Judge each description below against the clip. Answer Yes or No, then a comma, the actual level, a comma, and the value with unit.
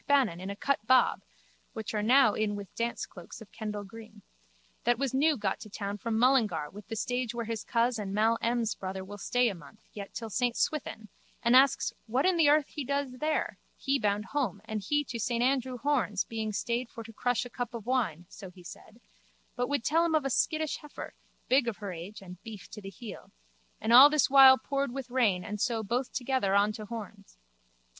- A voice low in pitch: No, high, 230 Hz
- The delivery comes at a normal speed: No, fast, 215 wpm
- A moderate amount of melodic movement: Yes, average, 4.1 semitones